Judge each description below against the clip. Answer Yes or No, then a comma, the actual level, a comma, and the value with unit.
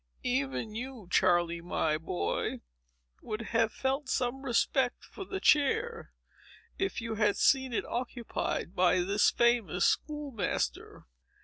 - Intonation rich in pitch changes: Yes, wide, 6.7 semitones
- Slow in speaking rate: Yes, slow, 125 wpm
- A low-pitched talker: No, high, 230 Hz